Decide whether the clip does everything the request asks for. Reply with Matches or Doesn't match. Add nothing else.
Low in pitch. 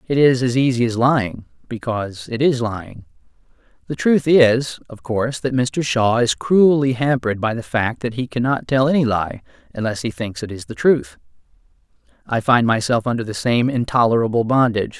Matches